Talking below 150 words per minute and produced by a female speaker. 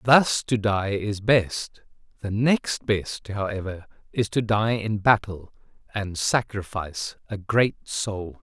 No: slow, 135 wpm; male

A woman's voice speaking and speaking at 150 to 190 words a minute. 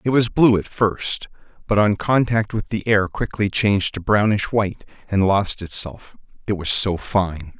No: male; average, 180 wpm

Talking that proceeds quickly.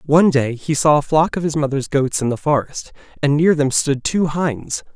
Yes: fast, 230 wpm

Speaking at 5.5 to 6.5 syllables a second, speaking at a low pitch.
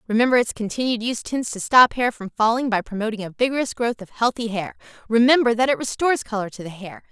No: 6.4 syllables/s; high, 230 Hz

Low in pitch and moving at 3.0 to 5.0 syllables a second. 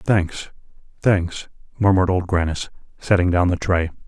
Yes: very low, 90 Hz; 4.5 syllables/s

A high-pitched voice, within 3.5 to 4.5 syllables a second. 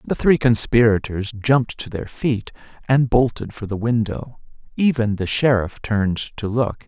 No: low, 115 Hz; 4.4 syllables/s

